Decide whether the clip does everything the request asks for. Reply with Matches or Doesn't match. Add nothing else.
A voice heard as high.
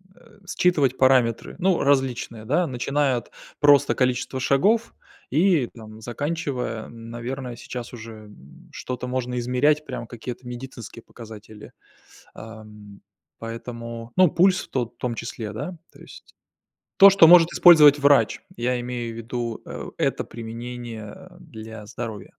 Doesn't match